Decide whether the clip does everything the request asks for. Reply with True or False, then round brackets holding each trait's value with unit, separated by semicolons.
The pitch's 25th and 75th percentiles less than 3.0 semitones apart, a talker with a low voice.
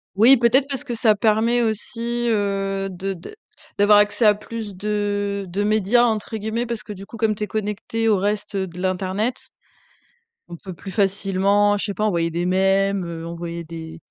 False (2.4 semitones; 205 Hz)